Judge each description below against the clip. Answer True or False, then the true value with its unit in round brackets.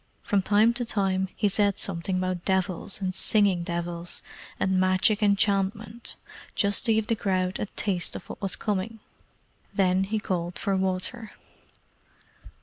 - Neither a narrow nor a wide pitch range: False (2.1 semitones)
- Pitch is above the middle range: True (195 Hz)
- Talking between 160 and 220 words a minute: False (145 wpm)